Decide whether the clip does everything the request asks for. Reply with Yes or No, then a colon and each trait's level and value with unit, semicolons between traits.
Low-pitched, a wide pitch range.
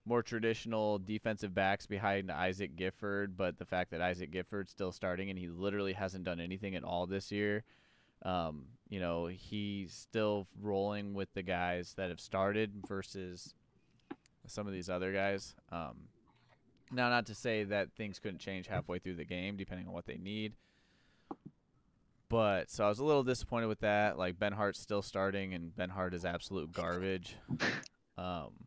No: very low, 95 Hz; narrow, 2.4 semitones